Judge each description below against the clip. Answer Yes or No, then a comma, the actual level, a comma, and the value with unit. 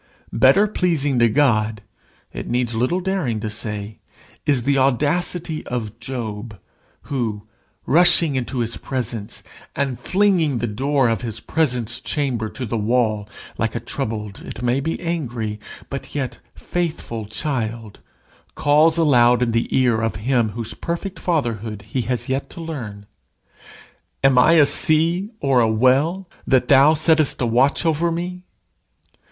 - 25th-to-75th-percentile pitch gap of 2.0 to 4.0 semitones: No, average, 5.3 semitones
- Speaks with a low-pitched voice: Yes, low, 125 Hz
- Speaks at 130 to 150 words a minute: Yes, average, 145 wpm